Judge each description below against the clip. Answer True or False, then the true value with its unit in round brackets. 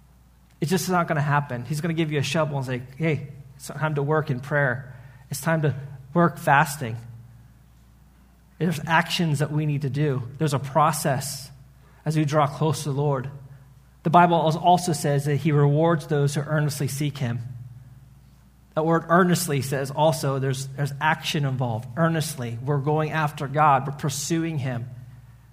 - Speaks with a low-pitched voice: False (145 Hz)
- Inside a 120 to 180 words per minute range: True (175 wpm)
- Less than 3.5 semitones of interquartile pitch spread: True (2.9 semitones)